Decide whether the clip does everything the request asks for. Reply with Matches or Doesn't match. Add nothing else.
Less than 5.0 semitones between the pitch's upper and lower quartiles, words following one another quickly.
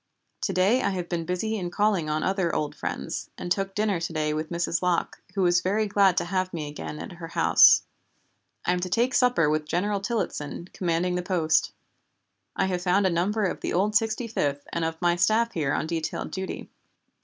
Matches